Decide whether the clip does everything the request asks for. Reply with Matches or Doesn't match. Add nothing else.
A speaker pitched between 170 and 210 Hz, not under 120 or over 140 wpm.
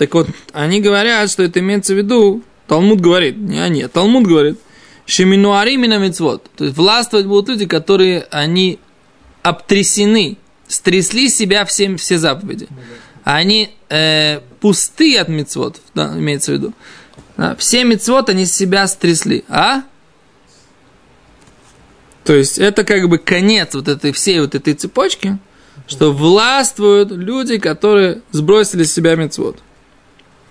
Matches